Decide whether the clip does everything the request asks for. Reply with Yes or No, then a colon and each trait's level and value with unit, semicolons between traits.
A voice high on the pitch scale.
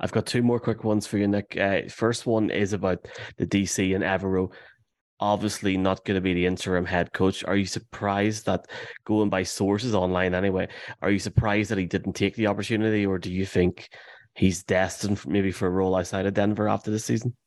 No: low, 100 Hz